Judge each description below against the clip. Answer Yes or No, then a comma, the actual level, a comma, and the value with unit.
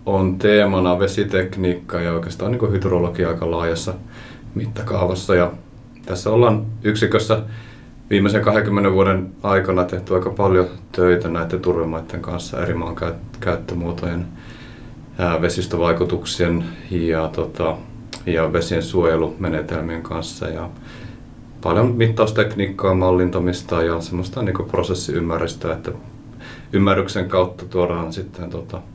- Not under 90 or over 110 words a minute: Yes, average, 100 wpm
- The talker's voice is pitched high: No, very low, 95 Hz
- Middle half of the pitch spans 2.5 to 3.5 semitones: No, average, 3.9 semitones